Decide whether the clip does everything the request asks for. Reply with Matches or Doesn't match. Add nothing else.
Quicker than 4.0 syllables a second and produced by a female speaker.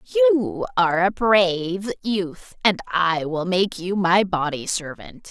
Doesn't match